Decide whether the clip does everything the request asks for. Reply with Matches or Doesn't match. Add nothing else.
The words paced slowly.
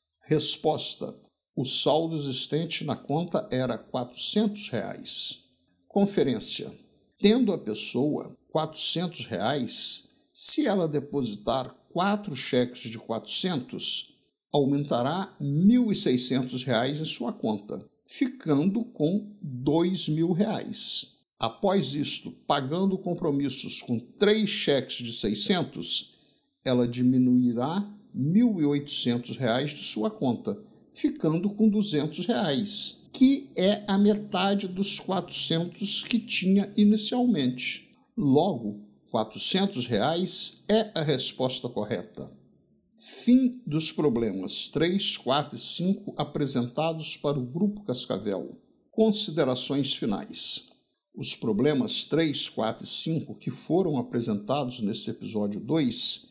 Matches